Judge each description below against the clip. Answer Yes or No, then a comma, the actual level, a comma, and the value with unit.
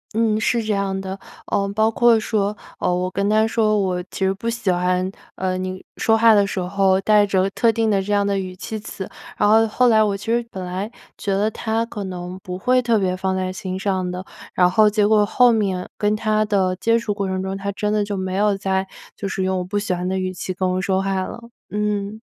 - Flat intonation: Yes, narrow, 2.3 semitones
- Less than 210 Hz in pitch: Yes, high, 200 Hz